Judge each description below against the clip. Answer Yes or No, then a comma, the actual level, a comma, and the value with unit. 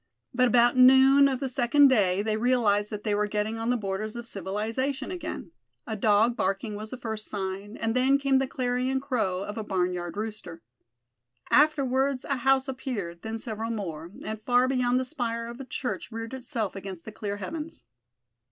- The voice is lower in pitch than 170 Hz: No, high, 230 Hz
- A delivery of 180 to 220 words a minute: Yes, average, 185 wpm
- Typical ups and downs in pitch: Yes, average, 3.9 semitones